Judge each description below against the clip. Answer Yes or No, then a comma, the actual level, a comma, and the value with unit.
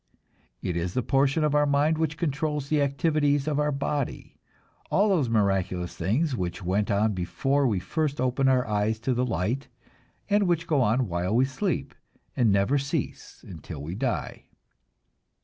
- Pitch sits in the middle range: No, low, 130 Hz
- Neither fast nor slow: Yes, average, 165 wpm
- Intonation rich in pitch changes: Yes, wide, 6.2 semitones